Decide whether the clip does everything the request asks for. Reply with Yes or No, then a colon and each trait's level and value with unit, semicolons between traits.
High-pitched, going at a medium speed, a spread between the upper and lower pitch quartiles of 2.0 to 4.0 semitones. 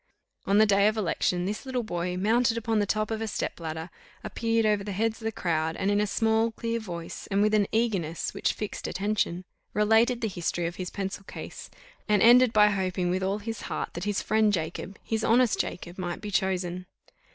No: high, 205 Hz; fast, 210 wpm; average, 3.4 semitones